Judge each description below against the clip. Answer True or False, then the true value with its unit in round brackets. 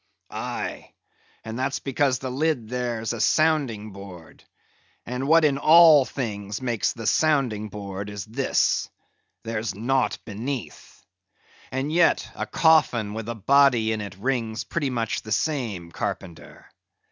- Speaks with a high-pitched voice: False (120 Hz)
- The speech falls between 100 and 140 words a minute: True (135 wpm)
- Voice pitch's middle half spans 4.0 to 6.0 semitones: True (4.4 semitones)